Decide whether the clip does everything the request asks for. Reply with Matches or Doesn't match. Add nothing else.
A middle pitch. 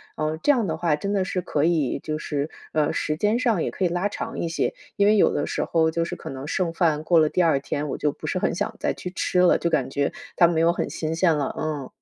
Matches